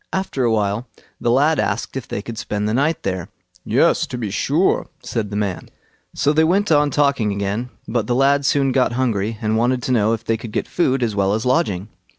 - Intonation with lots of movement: No, average, 4.9 semitones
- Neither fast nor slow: No, fast, 220 wpm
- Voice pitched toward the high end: No, low, 120 Hz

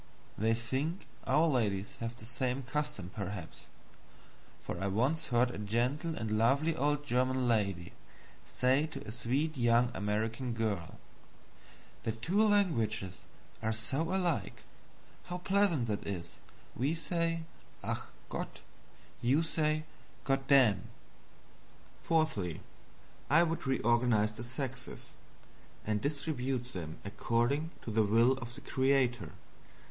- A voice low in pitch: Yes, low, 125 Hz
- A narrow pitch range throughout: No, average, 5.2 semitones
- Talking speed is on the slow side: Yes, slow, 120 wpm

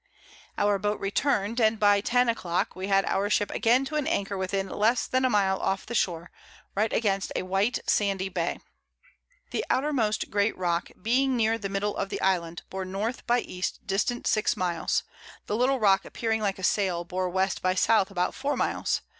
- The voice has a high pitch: Yes, high, 200 Hz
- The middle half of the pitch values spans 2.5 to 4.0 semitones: Yes, average, 3.1 semitones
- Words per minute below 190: No, average, 195 wpm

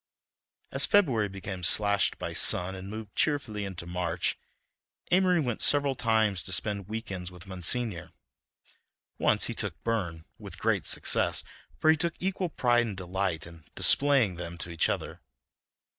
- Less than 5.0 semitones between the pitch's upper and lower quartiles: No, wide, 5.5 semitones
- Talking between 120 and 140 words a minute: No, average, 155 wpm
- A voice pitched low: Yes, low, 100 Hz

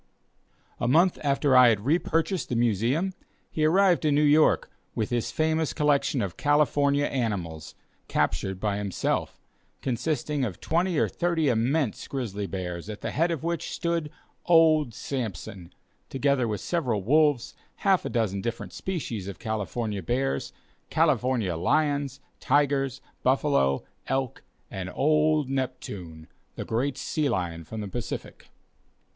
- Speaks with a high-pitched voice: No, low, 130 Hz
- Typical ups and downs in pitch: No, wide, 6.2 semitones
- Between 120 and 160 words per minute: Yes, average, 140 wpm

